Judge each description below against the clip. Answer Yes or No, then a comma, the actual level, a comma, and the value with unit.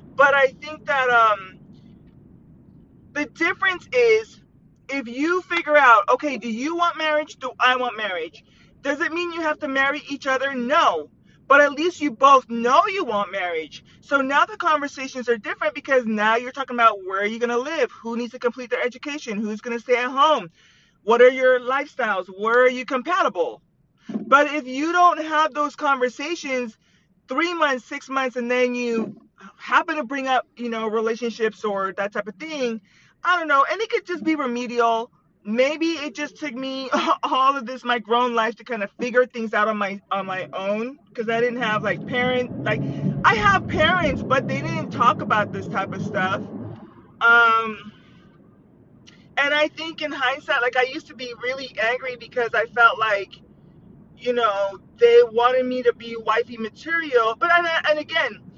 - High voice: Yes, very high, 255 Hz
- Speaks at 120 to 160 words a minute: No, average, 185 wpm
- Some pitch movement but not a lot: Yes, average, 4.4 semitones